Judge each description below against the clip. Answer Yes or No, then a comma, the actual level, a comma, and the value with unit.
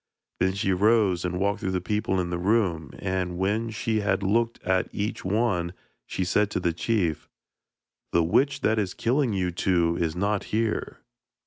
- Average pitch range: Yes, average, 3.4 semitones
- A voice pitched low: Yes, very low, 95 Hz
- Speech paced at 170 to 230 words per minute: Yes, average, 180 wpm